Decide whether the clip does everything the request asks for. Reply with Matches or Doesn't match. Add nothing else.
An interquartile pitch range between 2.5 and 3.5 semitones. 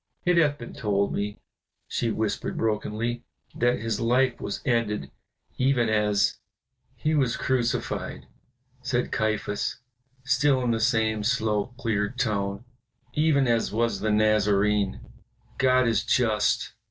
Matches